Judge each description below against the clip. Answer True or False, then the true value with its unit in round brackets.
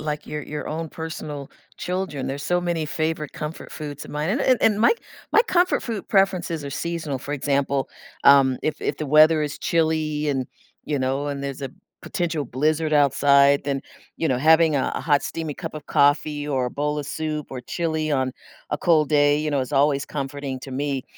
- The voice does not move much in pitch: True (2.2 semitones)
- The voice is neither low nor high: True (150 Hz)